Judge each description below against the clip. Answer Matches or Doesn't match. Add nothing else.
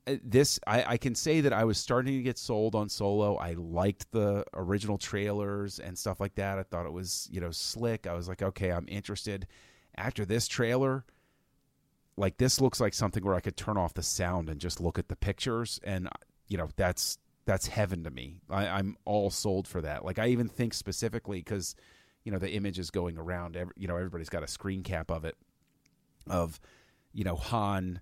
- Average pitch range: Matches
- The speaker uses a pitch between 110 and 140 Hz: Doesn't match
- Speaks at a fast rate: Matches